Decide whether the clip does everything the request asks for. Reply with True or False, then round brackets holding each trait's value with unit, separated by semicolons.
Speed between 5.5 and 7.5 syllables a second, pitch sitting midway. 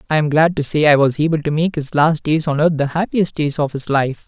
True (5.7 syllables/s; 150 Hz)